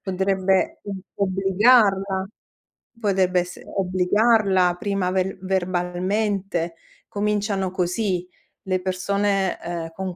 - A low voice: No, high, 190 Hz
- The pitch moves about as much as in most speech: No, narrow, 1.6 semitones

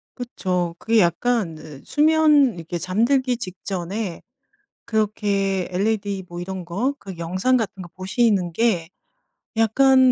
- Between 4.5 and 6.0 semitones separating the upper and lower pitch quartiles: Yes, average, 5.1 semitones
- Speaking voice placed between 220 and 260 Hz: No, high, 200 Hz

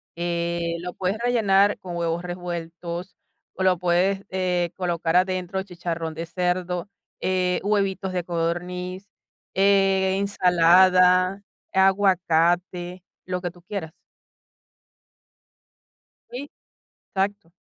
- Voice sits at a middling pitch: Yes, medium, 180 Hz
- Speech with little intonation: Yes, narrow, 1.7 semitones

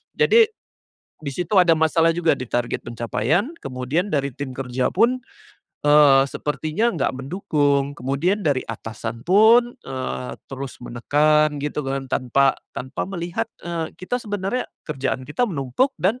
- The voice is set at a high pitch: No, medium, 150 Hz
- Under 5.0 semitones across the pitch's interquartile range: No, wide, 5.4 semitones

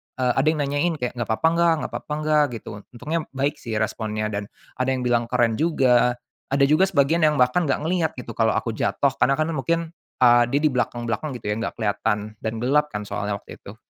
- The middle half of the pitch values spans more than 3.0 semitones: Yes, average, 4.8 semitones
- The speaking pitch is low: Yes, low, 130 Hz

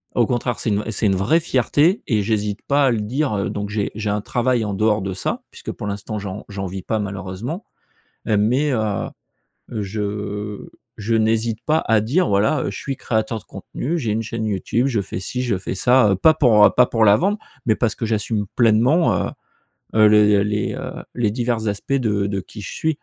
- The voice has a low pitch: Yes, low, 110 Hz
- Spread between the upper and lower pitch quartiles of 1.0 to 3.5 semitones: Yes, average, 3.1 semitones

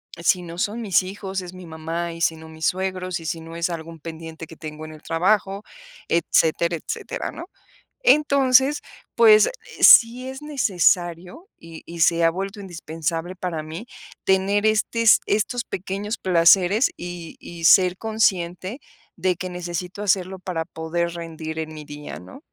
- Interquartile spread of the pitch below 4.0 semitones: Yes, average, 3.6 semitones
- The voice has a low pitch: No, medium, 180 Hz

